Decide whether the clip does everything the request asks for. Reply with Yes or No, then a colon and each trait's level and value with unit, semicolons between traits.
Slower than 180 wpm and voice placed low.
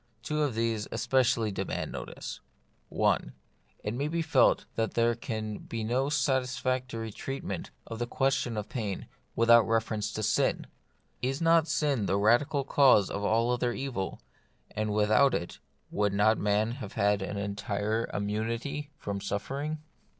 Yes: average, 155 wpm; low, 115 Hz